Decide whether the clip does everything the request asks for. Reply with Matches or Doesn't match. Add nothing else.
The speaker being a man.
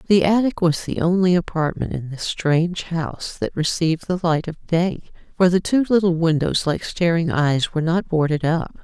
Doesn't match